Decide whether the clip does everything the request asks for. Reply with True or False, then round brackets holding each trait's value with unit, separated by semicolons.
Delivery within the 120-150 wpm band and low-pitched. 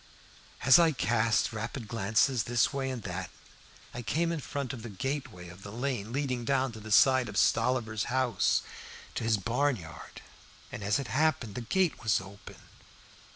False (165 wpm; 120 Hz)